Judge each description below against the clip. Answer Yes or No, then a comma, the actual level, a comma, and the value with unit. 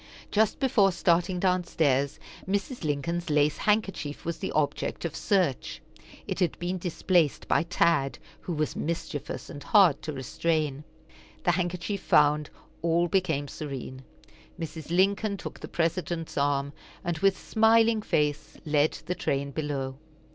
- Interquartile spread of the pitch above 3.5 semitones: Yes, average, 4.0 semitones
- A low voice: No, medium, 165 Hz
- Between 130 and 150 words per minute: Yes, slow, 135 wpm